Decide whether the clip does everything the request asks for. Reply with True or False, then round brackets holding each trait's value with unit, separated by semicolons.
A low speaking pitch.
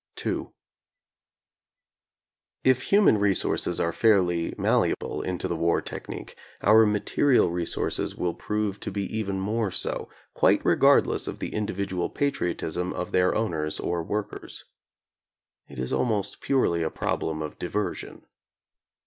True (95 Hz)